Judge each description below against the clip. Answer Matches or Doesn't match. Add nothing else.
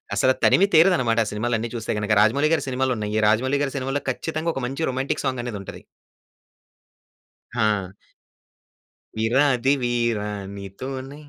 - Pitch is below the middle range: Matches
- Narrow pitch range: Doesn't match